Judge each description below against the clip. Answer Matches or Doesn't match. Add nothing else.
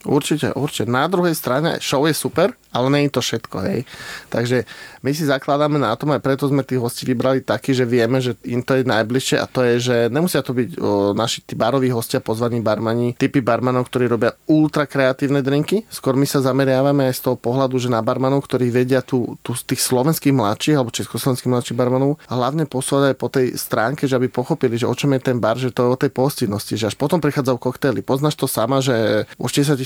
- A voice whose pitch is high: Doesn't match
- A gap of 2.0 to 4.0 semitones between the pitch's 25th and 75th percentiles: Matches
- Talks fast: Matches